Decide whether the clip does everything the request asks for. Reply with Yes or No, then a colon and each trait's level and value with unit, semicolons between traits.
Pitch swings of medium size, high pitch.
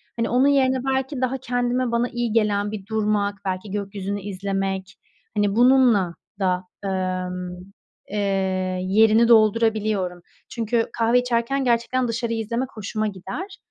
Yes: average, 3.6 semitones; high, 220 Hz